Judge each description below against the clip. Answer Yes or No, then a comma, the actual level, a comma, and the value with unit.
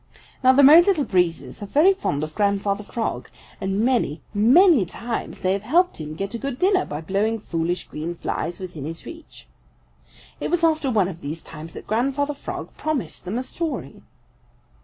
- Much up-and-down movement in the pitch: Yes, wide, 8.5 semitones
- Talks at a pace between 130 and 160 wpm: No, average, 180 wpm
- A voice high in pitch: Yes, high, 215 Hz